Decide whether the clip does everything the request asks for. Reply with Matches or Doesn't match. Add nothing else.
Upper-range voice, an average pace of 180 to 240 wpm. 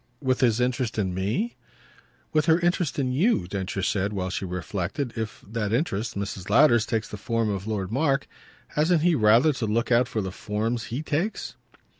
Doesn't match